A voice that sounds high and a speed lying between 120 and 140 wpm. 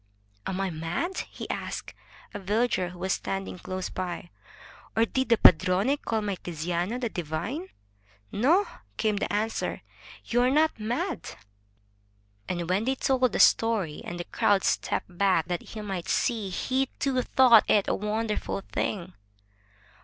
No: high, 205 Hz; average, 155 wpm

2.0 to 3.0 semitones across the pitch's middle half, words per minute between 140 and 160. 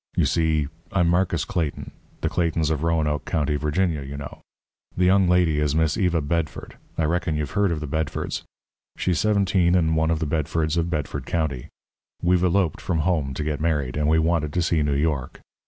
No: narrow, 2.5 semitones; average, 195 wpm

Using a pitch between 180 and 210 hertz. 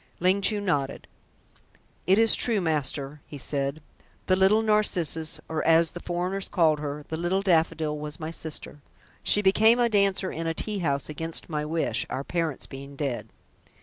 No: medium, 165 Hz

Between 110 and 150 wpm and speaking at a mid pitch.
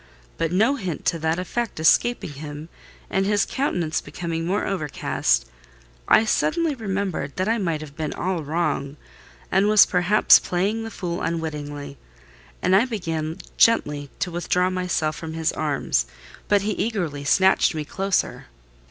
Yes: average, 145 wpm; medium, 175 Hz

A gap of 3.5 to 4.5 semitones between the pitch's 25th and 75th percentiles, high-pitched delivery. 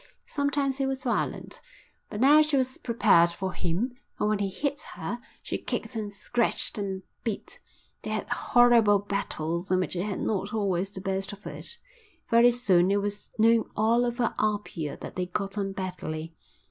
Yes: average, 4.0 semitones; high, 205 Hz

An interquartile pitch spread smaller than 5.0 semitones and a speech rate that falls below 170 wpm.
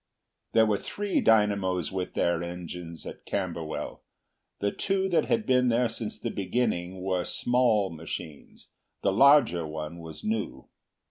No: average, 5.3 semitones; average, 140 wpm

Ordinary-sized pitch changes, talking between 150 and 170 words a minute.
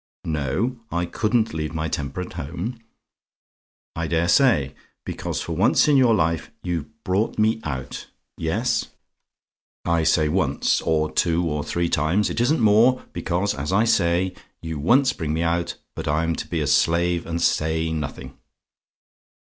Yes: average, 4.6 semitones; average, 155 wpm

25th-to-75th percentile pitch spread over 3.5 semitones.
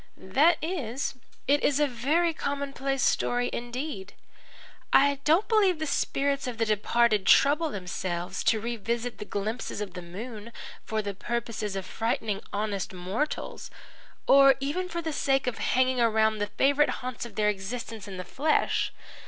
Yes: average, 5.2 semitones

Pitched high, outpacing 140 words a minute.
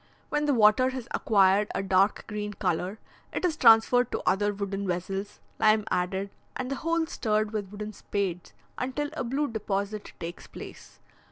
Yes: high, 210 Hz; average, 165 wpm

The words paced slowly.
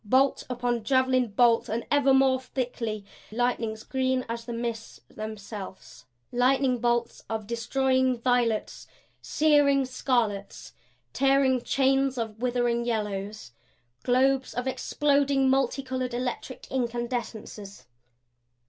Yes: slow, 105 wpm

